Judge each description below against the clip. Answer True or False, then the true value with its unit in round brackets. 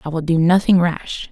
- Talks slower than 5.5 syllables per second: True (5.0 syllables/s)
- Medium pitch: True (170 Hz)